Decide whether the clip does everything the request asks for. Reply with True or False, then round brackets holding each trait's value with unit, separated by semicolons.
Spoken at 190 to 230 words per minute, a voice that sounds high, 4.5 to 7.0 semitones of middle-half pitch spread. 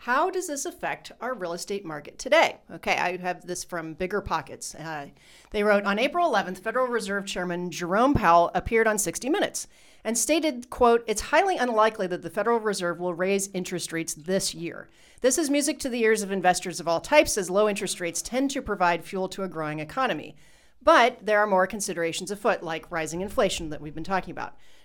True (205 wpm; 195 Hz; 5.1 semitones)